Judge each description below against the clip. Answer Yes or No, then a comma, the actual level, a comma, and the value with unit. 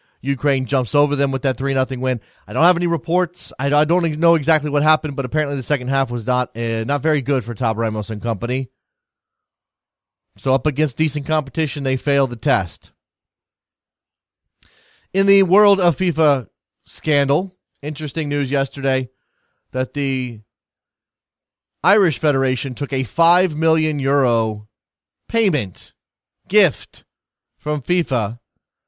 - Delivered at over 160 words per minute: No, average, 145 wpm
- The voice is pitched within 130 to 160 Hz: Yes, medium, 140 Hz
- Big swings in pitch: No, average, 3.6 semitones